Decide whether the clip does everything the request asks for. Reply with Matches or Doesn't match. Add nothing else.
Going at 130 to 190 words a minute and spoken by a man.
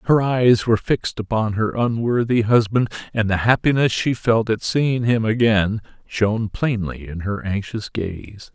Matches